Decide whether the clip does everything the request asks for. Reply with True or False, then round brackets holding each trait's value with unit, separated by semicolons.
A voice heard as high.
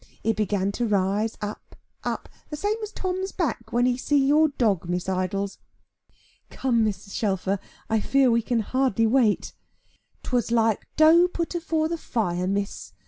True (230 Hz)